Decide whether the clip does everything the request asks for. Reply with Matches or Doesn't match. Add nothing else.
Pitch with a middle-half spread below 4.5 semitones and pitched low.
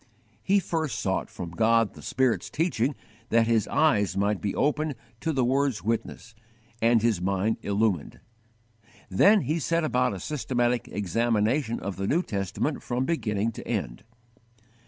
Doesn't match